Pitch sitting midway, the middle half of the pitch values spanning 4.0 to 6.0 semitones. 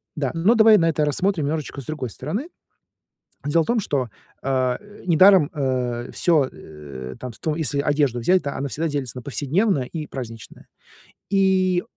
Yes: medium, 150 Hz; wide, 5.6 semitones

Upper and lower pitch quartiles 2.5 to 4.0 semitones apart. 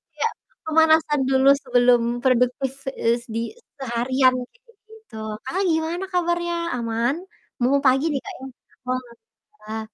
No: average, 4.7 semitones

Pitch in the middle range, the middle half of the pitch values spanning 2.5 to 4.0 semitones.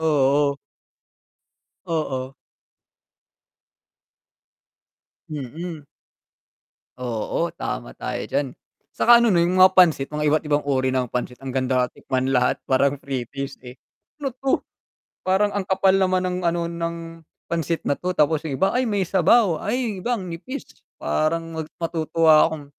No: medium, 160 Hz; average, 5.0 semitones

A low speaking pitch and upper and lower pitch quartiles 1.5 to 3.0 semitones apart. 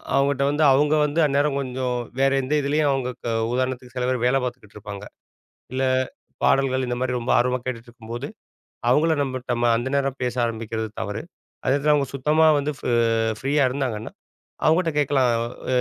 Yes: low, 130 Hz; narrow, 2.5 semitones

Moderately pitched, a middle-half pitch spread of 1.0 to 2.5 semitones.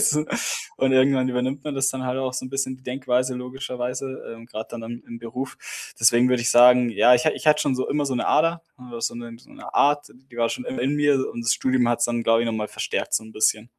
No: low, 125 Hz; narrow, 2.2 semitones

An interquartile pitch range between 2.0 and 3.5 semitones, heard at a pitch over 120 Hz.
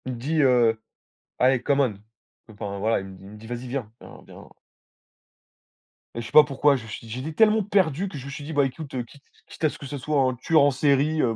No: average, 3.9 semitones; low, 135 Hz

